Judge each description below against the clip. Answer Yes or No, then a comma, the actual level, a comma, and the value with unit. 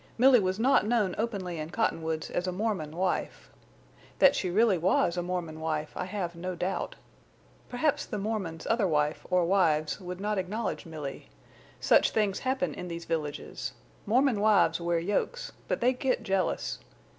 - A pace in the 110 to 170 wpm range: Yes, average, 165 wpm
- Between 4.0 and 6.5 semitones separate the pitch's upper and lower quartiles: Yes, average, 4.6 semitones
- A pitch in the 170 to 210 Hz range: Yes, medium, 185 Hz